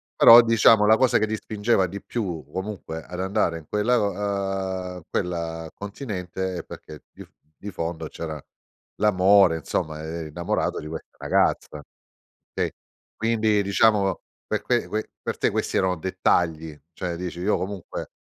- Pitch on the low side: Yes, very low, 95 Hz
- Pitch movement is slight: No, average, 3.7 semitones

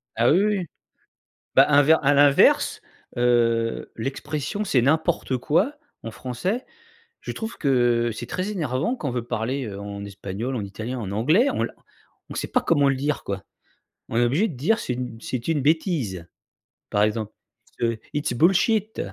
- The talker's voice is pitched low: Yes, low, 130 Hz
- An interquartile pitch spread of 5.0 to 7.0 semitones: Yes, wide, 5.6 semitones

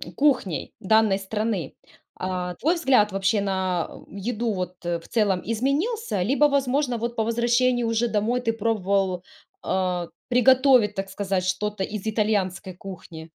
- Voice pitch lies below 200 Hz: No, high, 210 Hz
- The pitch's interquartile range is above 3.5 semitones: Yes, average, 4.2 semitones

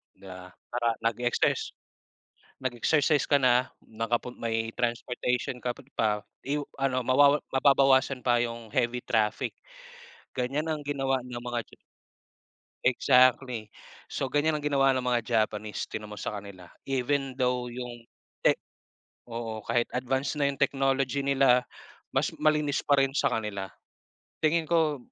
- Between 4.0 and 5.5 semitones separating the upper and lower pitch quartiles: No, average, 2.7 semitones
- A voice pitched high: No, low, 125 Hz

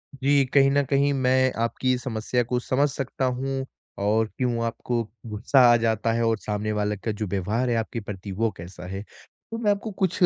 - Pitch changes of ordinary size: Yes, average, 3.8 semitones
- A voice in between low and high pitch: No, low, 120 Hz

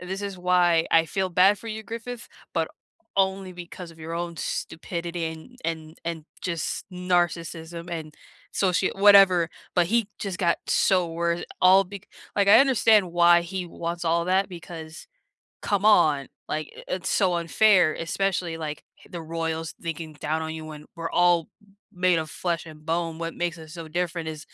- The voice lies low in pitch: No, medium, 170 Hz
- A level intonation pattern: Yes, narrow, 2.3 semitones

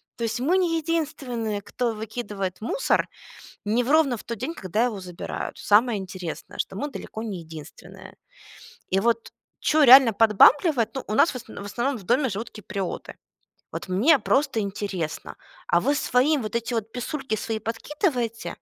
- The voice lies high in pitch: Yes, high, 230 Hz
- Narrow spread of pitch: No, average, 4.7 semitones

